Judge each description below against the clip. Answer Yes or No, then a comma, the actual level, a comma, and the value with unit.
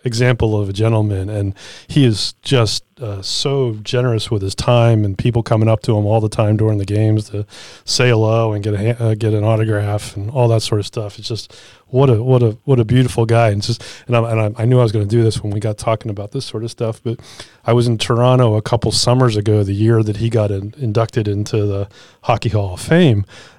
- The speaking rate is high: Yes, fast, 245 wpm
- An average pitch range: No, narrow, 2.2 semitones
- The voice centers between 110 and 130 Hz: Yes, low, 115 Hz